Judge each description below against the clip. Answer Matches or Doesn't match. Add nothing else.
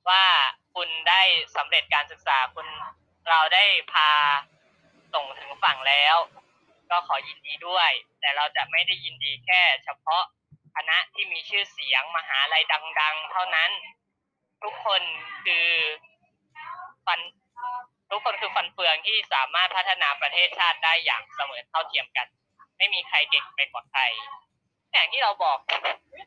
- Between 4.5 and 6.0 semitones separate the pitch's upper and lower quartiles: Doesn't match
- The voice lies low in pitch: Doesn't match